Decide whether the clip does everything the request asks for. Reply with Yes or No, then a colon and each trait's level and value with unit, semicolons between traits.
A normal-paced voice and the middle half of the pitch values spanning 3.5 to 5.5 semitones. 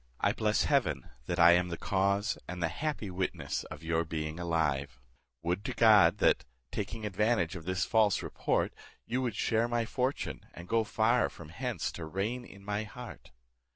Yes: average, 180 wpm; average, 4.8 semitones